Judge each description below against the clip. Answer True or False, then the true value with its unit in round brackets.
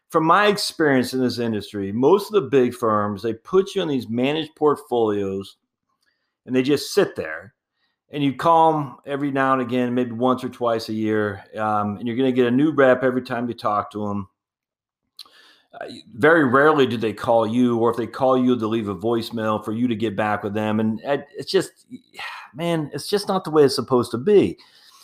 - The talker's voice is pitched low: True (125 Hz)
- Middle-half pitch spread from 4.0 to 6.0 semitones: True (4.3 semitones)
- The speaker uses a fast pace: True (210 wpm)